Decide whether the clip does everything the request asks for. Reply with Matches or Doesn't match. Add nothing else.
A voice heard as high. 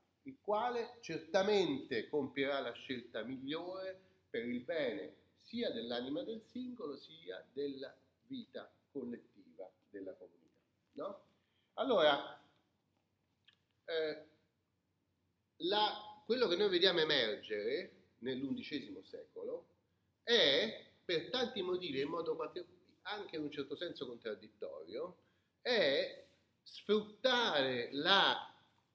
Matches